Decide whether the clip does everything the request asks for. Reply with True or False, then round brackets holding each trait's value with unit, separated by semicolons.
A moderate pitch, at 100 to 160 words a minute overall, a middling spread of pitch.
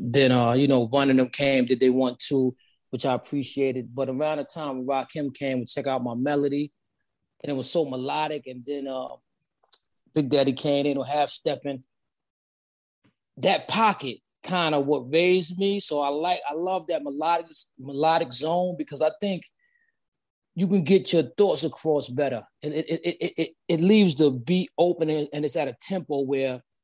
False (145 Hz; 195 wpm; 3.7 semitones)